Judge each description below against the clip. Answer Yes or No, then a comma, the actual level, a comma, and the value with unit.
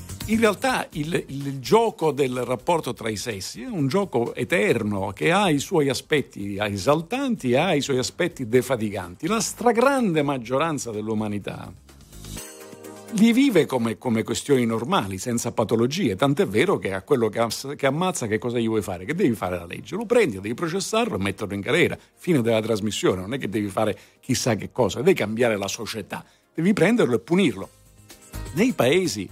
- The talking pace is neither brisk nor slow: No, fast, 175 wpm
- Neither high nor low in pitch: No, low, 120 Hz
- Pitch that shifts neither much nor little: No, wide, 7.8 semitones